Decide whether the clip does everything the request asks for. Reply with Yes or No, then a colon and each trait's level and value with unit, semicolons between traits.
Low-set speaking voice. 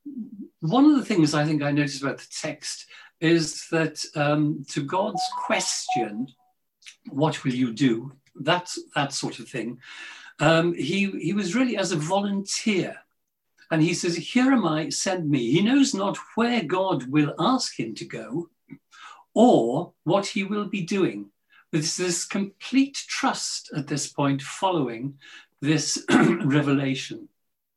No: medium, 175 Hz